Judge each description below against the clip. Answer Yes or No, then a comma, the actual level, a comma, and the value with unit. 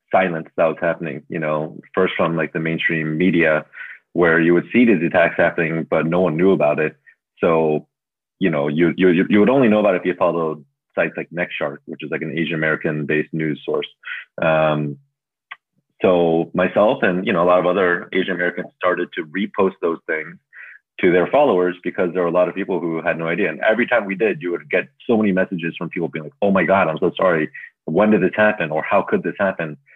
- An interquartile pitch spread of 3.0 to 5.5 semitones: No, narrow, 2.4 semitones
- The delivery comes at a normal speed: No, fast, 225 wpm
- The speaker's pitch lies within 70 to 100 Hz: Yes, very low, 85 Hz